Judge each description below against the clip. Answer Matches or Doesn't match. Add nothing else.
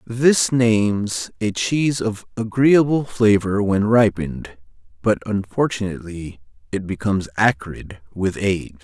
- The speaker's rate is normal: Doesn't match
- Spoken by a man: Matches